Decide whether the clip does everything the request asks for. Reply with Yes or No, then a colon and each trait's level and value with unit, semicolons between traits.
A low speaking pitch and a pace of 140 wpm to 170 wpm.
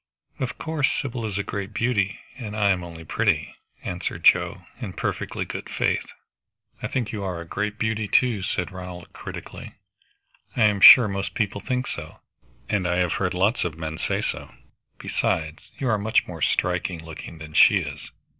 No: low, 100 Hz; average, 180 wpm